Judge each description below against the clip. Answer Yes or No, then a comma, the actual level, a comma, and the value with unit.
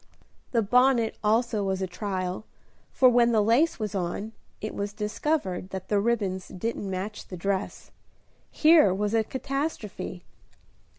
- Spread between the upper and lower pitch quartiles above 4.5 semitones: No, average, 3.7 semitones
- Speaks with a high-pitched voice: Yes, high, 210 Hz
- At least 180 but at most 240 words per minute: No, average, 140 wpm